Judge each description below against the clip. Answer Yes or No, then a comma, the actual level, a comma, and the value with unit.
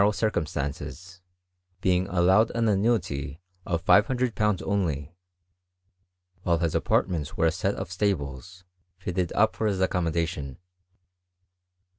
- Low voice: Yes, very low, 90 Hz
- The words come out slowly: Yes, slow, 110 wpm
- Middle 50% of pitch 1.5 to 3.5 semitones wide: No, average, 4.0 semitones